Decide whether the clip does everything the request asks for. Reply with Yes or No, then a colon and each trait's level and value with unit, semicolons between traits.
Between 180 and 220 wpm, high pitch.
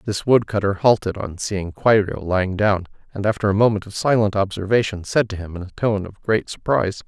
No: fast, 205 wpm; low, 100 Hz